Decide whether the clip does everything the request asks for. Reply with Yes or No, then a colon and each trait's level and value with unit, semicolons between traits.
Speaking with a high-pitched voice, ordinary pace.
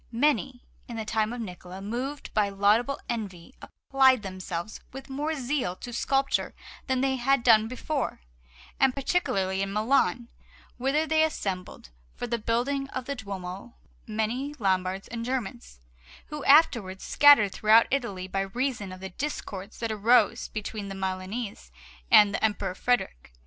Yes: high, 230 Hz; average, 150 wpm